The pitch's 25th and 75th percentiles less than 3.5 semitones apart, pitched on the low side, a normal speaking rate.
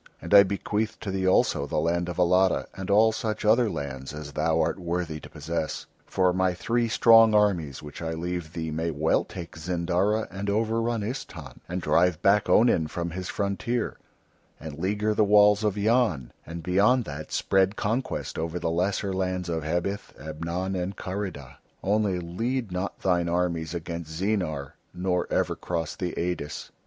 No: average, 3.8 semitones; very low, 90 Hz; average, 170 wpm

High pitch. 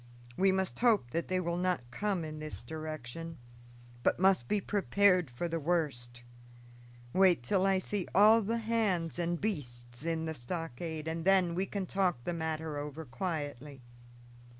No: medium, 165 Hz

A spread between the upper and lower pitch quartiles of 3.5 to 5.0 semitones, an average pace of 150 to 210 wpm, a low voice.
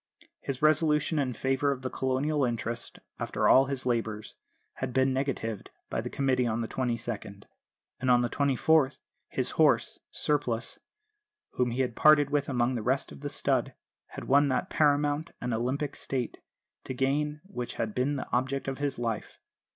No: average, 2.8 semitones; average, 170 wpm; low, 130 Hz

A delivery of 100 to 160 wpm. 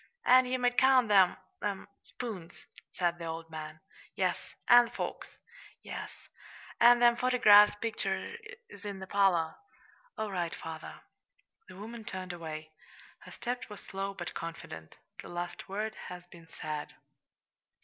Yes: average, 140 wpm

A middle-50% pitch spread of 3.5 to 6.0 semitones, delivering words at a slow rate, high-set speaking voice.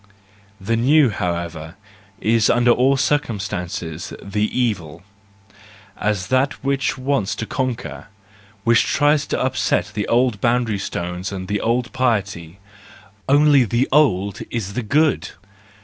No: average, 5.1 semitones; slow, 130 wpm; low, 115 Hz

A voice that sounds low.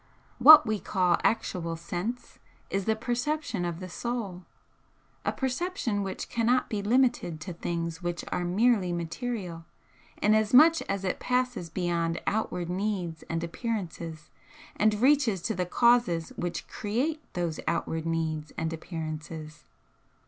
No: medium, 185 Hz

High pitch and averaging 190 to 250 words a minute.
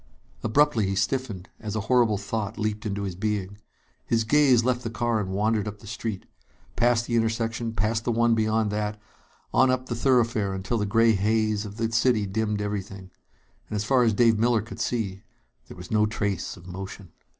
No: low, 110 Hz; average, 195 wpm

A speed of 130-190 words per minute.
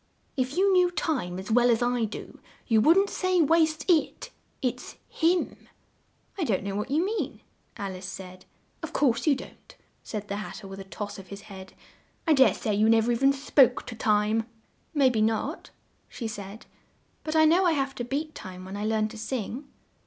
No: fast, 205 wpm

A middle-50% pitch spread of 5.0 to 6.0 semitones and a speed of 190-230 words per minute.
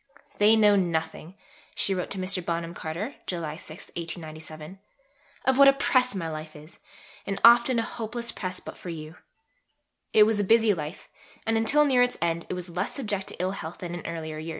Yes: average, 5.3 semitones; average, 195 wpm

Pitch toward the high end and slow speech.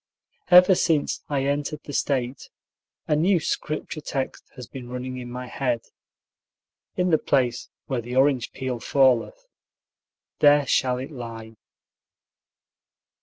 No: low, 135 Hz; slow, 130 wpm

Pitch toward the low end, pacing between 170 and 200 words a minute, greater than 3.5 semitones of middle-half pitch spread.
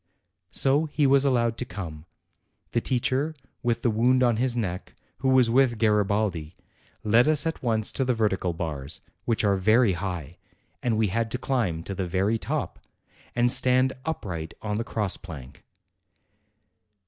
No: low, 110 Hz; average, 160 wpm; average, 5.0 semitones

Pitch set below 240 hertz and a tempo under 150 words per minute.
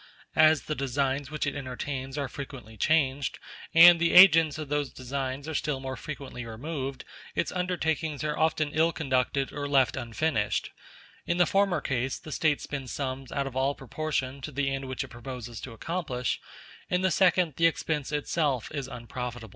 No: medium, 140 Hz; average, 175 wpm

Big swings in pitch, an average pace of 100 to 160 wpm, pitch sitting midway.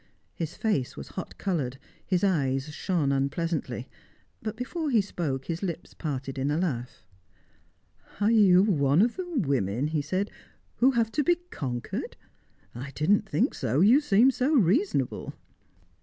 Yes: wide, 8.0 semitones; average, 150 wpm; medium, 175 Hz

